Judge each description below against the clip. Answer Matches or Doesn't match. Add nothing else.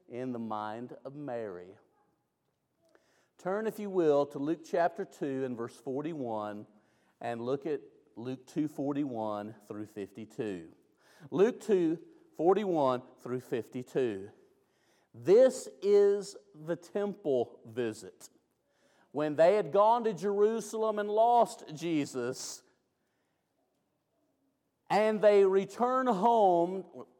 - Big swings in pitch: Matches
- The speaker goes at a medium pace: Doesn't match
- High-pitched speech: Doesn't match